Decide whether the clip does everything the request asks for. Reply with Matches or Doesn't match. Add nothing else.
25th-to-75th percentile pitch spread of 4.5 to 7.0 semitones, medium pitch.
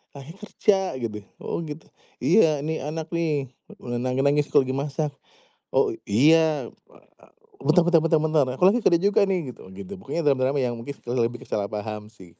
Matches